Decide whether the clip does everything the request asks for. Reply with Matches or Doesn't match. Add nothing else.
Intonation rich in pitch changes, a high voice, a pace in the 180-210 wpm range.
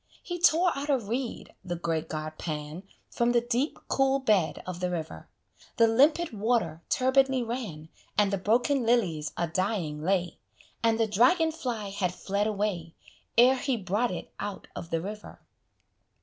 Doesn't match